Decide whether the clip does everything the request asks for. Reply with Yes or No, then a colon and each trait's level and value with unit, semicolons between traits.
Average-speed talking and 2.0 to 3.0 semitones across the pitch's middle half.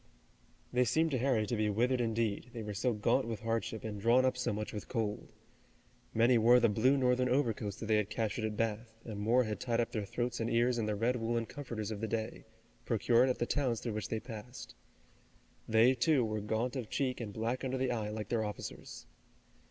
No: fast, 220 wpm; narrow, 2.4 semitones